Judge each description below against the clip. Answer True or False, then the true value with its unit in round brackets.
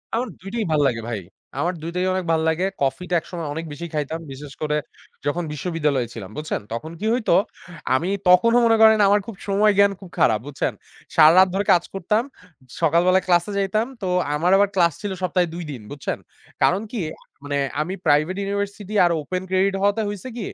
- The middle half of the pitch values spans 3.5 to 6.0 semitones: True (4.5 semitones)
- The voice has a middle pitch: True (180 Hz)